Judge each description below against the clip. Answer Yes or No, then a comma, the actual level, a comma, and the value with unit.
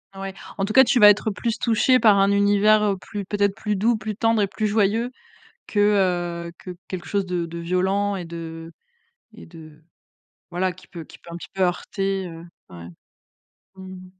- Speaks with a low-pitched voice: No, high, 195 Hz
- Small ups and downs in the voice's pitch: No, average, 3.2 semitones